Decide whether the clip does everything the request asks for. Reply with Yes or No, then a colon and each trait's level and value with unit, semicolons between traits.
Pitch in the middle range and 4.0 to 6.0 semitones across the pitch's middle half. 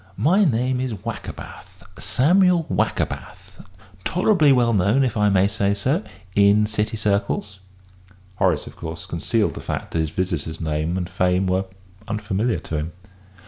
No: low, 100 Hz; average, 5.1 semitones